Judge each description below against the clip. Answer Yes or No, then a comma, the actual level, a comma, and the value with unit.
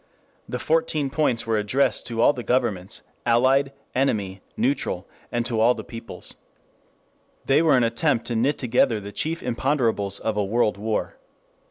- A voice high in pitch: No, low, 120 Hz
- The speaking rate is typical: Yes, average, 160 wpm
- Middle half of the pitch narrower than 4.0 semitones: Yes, average, 3.6 semitones